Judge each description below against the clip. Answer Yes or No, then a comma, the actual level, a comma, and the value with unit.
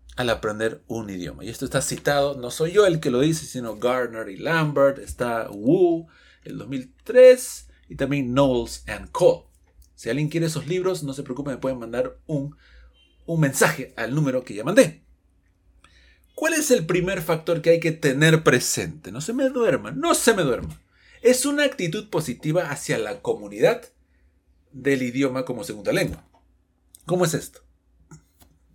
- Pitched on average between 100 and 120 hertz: No, medium, 140 Hz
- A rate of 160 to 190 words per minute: Yes, average, 165 wpm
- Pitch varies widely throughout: Yes, wide, 6.4 semitones